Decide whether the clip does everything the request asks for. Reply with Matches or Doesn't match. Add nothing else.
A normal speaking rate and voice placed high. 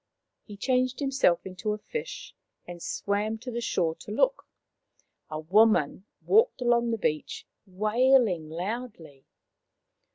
Doesn't match